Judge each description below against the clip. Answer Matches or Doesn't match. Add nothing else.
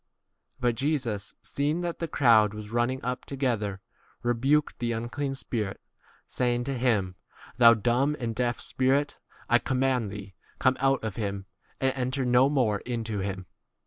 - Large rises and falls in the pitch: Doesn't match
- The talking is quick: Doesn't match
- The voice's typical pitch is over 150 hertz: Doesn't match